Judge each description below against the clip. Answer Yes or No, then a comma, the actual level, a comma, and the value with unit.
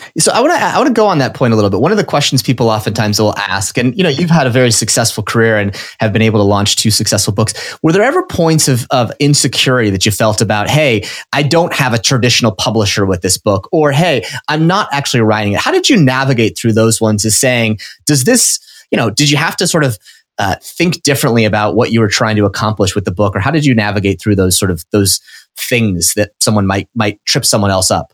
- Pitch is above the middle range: No, low, 115 Hz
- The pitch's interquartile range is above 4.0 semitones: Yes, average, 5.2 semitones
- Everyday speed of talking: No, fast, 250 wpm